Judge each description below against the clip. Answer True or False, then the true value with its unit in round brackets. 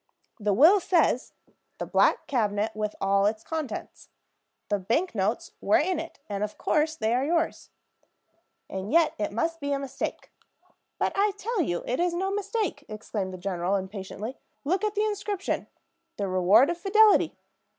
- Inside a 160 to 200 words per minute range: True (165 wpm)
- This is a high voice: True (270 Hz)